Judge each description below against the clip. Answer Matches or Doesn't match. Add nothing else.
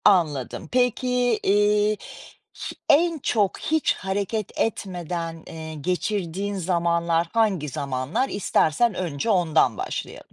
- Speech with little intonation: Doesn't match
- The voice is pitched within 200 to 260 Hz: Doesn't match